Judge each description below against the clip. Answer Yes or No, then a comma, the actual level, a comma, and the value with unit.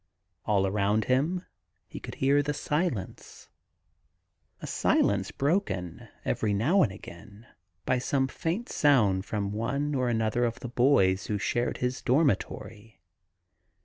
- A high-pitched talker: No, low, 120 Hz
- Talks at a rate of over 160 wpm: No, slow, 135 wpm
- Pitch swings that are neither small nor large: No, wide, 5.7 semitones